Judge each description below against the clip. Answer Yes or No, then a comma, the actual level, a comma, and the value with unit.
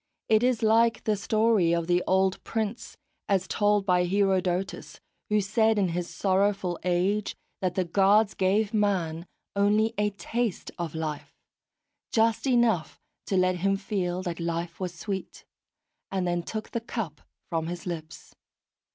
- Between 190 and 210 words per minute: No, average, 150 wpm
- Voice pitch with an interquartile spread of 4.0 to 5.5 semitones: No, average, 3.4 semitones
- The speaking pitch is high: Yes, high, 195 Hz